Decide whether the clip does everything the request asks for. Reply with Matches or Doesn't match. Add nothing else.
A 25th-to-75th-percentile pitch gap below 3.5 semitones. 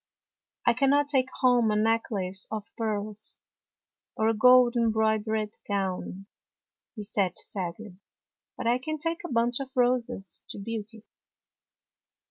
Matches